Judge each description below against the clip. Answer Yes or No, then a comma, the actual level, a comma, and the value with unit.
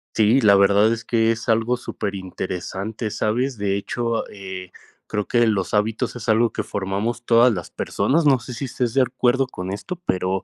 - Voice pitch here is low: Yes, low, 110 Hz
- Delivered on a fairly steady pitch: No, average, 3.3 semitones